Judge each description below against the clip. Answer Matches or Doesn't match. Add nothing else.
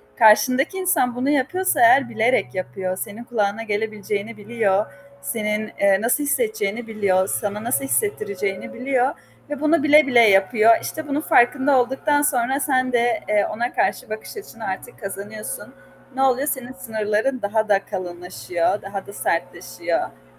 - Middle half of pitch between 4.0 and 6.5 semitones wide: Matches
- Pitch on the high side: Matches